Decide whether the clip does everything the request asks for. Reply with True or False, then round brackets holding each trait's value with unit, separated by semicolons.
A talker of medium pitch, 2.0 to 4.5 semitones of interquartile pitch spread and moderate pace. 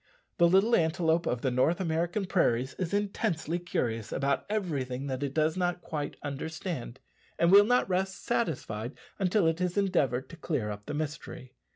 False (160 Hz; 5.3 semitones; 170 wpm)